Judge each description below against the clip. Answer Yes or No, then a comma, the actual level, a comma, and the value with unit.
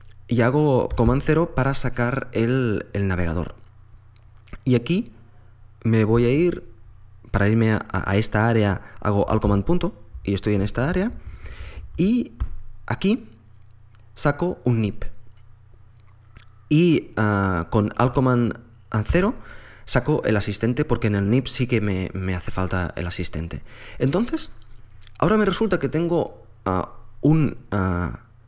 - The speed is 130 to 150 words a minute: Yes, average, 135 wpm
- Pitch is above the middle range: No, low, 110 Hz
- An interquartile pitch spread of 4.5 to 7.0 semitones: No, average, 3.4 semitones